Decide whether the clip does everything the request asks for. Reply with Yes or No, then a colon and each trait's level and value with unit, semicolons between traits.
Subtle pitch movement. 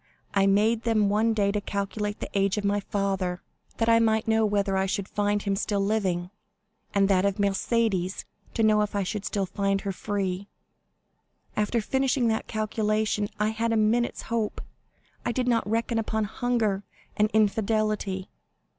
Yes: narrow, 1.9 semitones